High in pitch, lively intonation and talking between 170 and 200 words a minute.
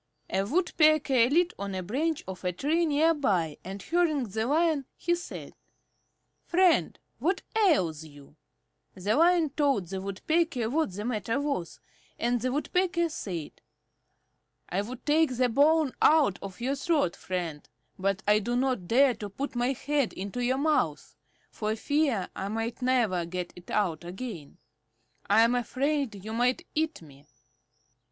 No: high, 245 Hz; wide, 7.6 semitones; average, 155 wpm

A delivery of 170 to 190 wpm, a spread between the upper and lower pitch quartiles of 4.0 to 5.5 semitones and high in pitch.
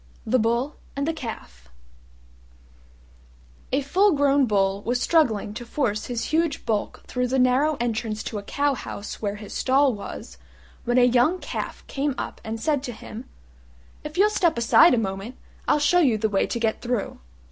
Yes: average, 180 wpm; average, 4.6 semitones; high, 245 Hz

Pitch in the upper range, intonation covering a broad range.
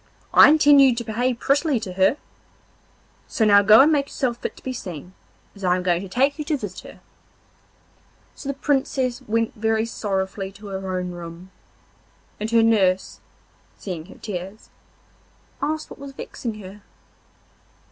Yes: high, 220 Hz; wide, 5.7 semitones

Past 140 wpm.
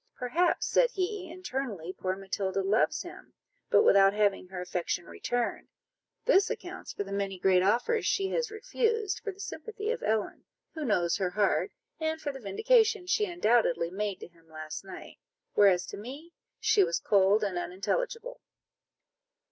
Yes: average, 160 wpm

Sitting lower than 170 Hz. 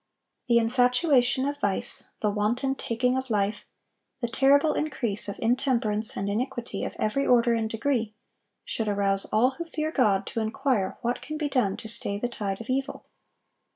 No: high, 235 Hz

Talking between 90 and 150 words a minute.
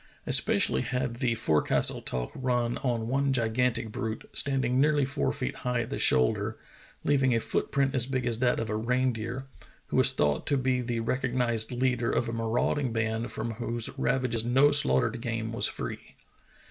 No: average, 175 wpm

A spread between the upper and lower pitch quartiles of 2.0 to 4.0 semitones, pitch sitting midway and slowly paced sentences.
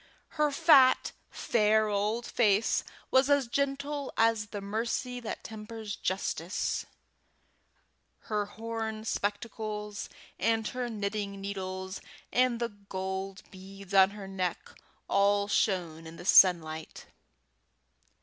No: average, 2.9 semitones; high, 210 Hz; slow, 110 wpm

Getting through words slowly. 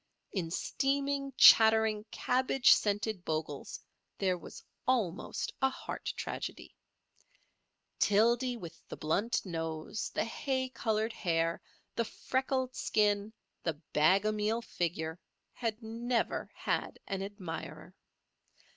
Yes: slow, 110 wpm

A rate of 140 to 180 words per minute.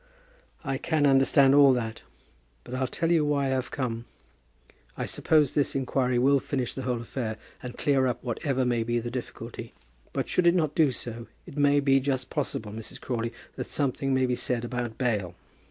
No: average, 190 wpm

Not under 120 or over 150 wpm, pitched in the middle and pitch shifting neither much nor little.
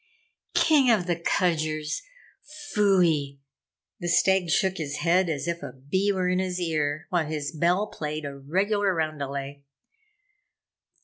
Yes: slow, 135 wpm; medium, 170 Hz; average, 3.8 semitones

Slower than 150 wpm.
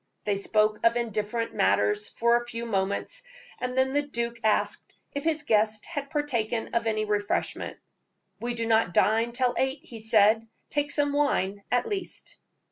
No: average, 165 wpm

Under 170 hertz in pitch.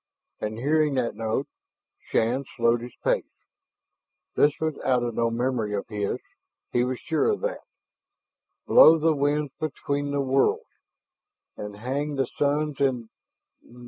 Yes: low, 135 Hz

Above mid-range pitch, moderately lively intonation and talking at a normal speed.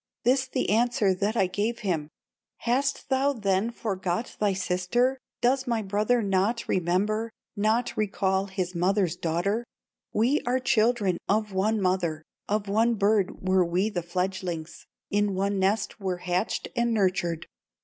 Yes: high, 200 Hz; average, 3.8 semitones; average, 145 wpm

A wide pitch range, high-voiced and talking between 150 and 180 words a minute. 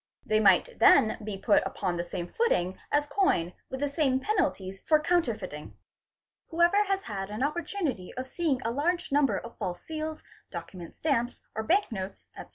Yes: wide, 8.6 semitones; very high, 255 Hz; average, 175 wpm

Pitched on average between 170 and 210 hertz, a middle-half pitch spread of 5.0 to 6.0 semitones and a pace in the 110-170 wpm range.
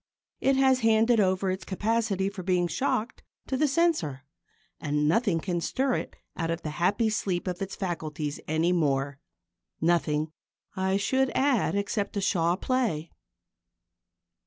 Yes: high, 190 Hz; wide, 5.4 semitones; average, 145 wpm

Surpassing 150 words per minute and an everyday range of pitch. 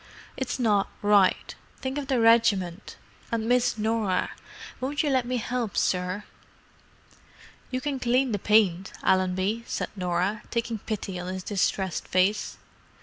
No: average, 140 wpm; average, 4.5 semitones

